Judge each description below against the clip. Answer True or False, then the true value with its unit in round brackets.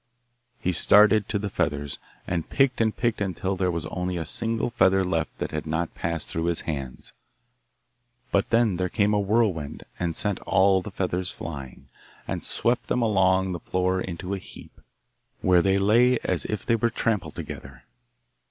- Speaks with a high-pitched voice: False (95 Hz)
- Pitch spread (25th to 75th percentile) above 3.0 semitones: True (3.8 semitones)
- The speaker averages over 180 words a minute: False (175 wpm)